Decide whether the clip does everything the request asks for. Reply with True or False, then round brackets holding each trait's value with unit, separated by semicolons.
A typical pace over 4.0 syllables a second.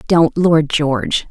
False (3.5 syllables/s)